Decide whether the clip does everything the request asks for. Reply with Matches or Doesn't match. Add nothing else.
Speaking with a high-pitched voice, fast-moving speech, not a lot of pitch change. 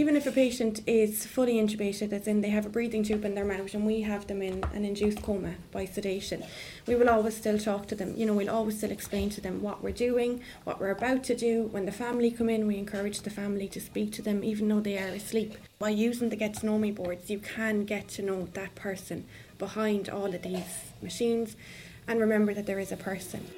Matches